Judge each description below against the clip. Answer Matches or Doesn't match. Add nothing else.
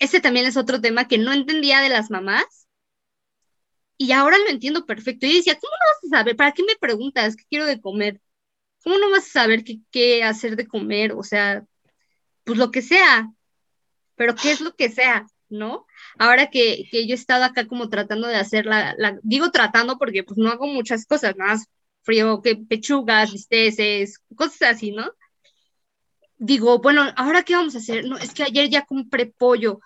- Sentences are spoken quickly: Matches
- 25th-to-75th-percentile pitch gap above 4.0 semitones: Matches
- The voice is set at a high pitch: Matches